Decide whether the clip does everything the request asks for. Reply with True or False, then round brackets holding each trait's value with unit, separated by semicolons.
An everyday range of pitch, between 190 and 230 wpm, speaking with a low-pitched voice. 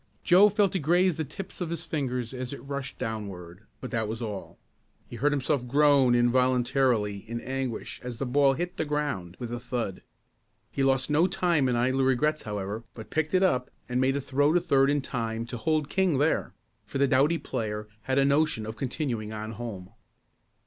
True (4.2 semitones; 195 wpm; 130 Hz)